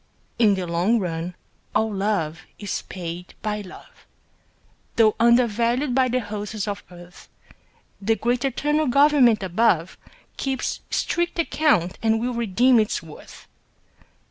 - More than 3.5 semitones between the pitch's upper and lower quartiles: Yes, average, 4.8 semitones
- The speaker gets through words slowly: Yes, slow, 125 wpm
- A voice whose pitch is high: Yes, high, 220 Hz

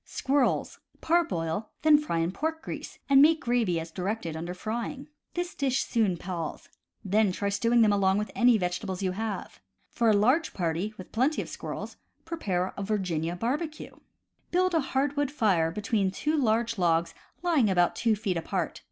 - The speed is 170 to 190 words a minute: Yes, average, 180 wpm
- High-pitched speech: Yes, high, 215 Hz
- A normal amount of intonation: No, wide, 6.9 semitones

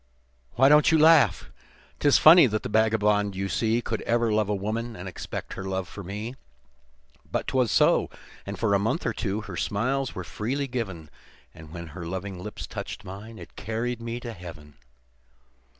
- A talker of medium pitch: No, low, 110 Hz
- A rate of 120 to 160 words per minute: No, average, 180 wpm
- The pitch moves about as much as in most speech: Yes, average, 3.8 semitones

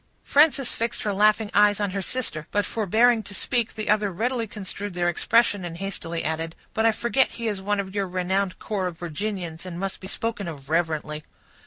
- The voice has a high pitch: Yes, high, 200 Hz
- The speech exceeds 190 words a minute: Yes, average, 200 wpm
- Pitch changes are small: No, average, 3.9 semitones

